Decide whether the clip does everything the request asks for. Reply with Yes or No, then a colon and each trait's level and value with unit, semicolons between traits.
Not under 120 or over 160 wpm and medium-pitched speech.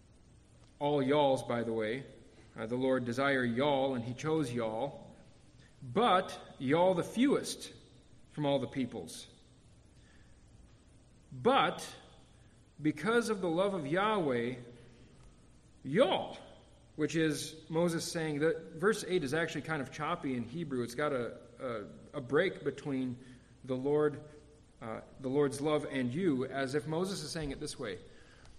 Yes: average, 140 wpm; medium, 145 Hz